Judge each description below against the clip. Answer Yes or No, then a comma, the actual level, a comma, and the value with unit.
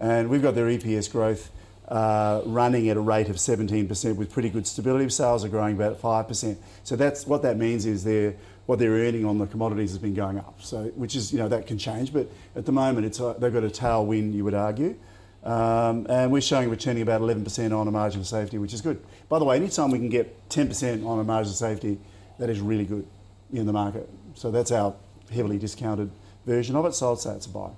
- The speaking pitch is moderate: No, low, 110 Hz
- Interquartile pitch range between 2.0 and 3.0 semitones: Yes, narrow, 2.4 semitones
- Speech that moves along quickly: Yes, fast, 240 wpm